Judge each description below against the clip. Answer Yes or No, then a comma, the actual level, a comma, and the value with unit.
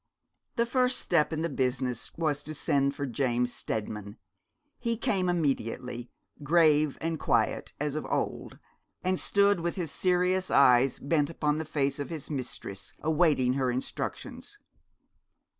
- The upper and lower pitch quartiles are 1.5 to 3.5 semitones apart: No, average, 4.7 semitones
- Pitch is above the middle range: No, medium, 150 Hz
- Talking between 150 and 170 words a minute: No, average, 140 wpm